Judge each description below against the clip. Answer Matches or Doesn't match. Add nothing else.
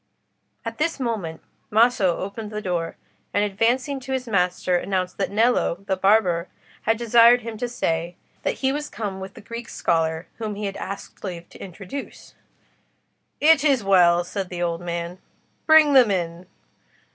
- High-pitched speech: Matches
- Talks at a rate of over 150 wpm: Matches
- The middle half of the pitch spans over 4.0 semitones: Matches